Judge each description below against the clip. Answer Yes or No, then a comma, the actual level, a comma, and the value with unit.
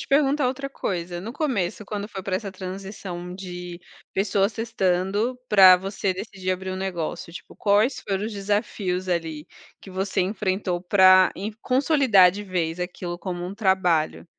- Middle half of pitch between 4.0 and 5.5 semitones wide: No, narrow, 2.5 semitones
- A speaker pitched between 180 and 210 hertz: Yes, high, 190 Hz